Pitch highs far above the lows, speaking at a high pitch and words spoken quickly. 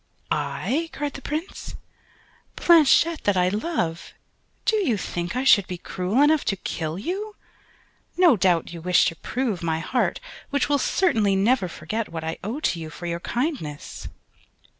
No: wide, 9.0 semitones; high, 215 Hz; average, 160 wpm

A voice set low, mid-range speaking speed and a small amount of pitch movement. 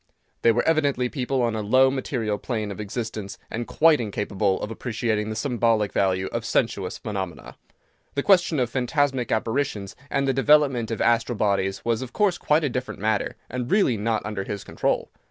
No: low, 115 Hz; average, 180 wpm; average, 3.9 semitones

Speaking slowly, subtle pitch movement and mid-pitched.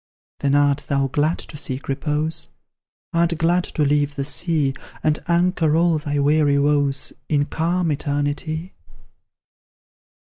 Yes: slow, 130 wpm; narrow, 2.3 semitones; medium, 150 Hz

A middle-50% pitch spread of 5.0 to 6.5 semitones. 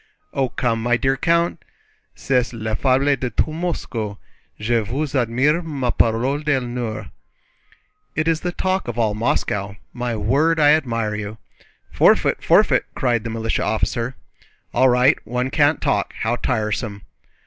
No: average, 4.2 semitones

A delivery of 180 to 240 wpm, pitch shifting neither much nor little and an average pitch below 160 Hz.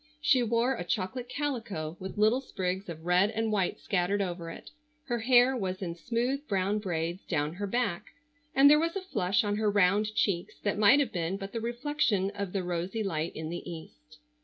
No: average, 200 wpm; average, 4.9 semitones; high, 200 Hz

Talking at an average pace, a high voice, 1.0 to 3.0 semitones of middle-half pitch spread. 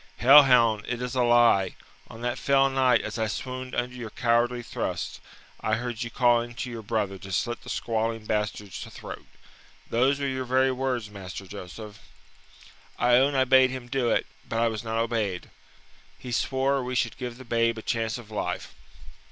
No: average, 185 wpm; low, 120 Hz; narrow, 2.5 semitones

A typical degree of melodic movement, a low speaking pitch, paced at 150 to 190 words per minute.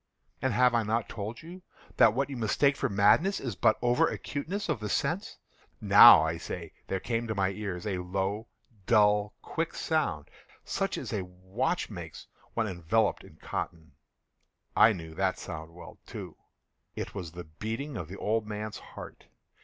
Yes: average, 4.5 semitones; low, 105 Hz; average, 170 wpm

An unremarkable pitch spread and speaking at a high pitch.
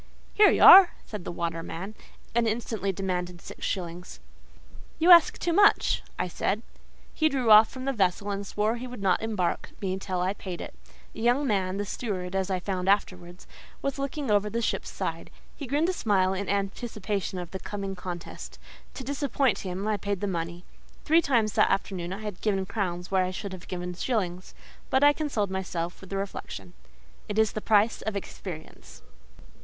Yes: average, 3.8 semitones; high, 200 Hz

